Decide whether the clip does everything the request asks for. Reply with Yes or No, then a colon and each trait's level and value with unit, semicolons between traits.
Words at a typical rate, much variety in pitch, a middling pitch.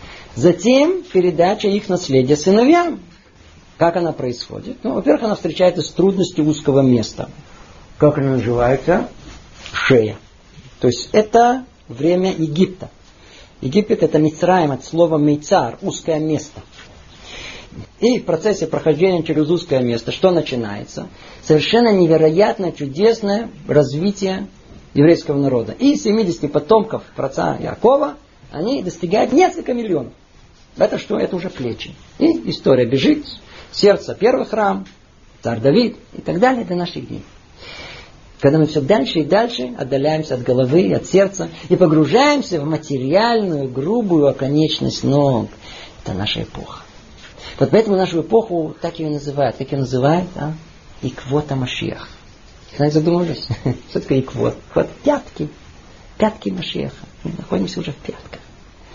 Yes: average, 125 wpm; wide, 5.8 semitones; medium, 165 Hz